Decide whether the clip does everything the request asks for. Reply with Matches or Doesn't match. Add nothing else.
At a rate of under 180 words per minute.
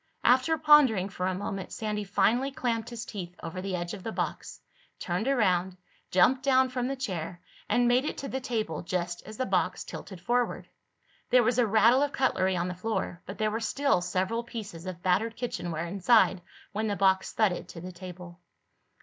Doesn't match